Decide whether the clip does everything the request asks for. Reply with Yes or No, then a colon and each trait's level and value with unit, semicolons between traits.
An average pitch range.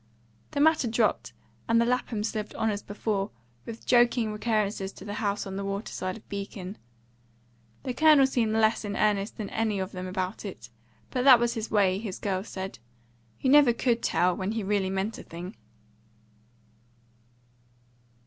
Yes: average, 3.0 semitones